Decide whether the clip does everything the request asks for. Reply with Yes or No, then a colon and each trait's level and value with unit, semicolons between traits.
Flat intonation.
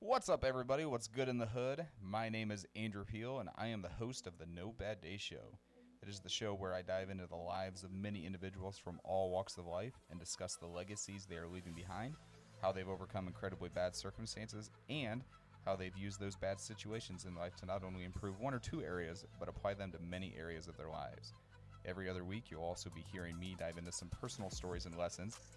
No: average, 3.3 semitones